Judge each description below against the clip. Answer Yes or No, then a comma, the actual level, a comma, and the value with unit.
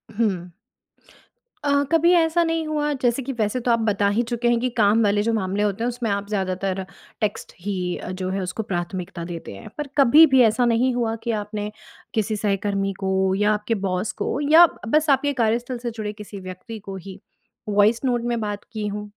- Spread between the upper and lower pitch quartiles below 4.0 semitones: Yes, average, 3.5 semitones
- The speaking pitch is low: No, high, 215 Hz